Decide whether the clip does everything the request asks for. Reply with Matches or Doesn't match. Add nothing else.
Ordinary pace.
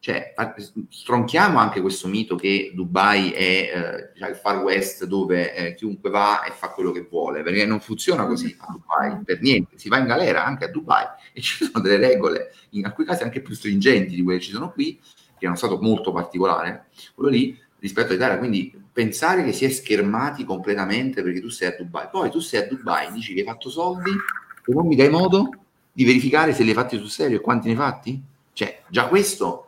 Doesn't match